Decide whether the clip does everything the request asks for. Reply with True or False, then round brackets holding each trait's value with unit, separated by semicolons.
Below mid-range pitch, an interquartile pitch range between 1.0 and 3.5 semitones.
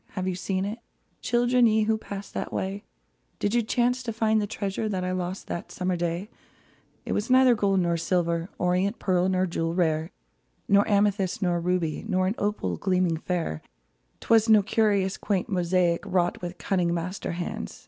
False (185 Hz; 3.0 semitones)